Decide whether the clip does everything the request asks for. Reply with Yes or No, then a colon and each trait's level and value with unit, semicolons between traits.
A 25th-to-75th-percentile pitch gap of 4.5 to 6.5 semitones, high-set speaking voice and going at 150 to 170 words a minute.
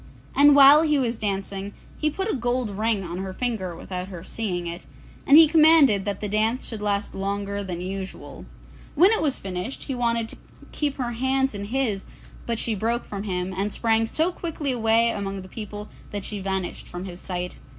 No: average, 4.9 semitones; high, 215 Hz; average, 200 wpm